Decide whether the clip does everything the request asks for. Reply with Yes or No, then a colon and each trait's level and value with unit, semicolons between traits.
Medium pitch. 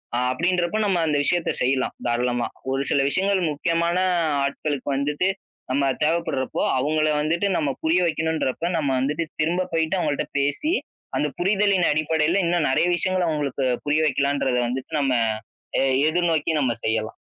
Yes: medium, 155 Hz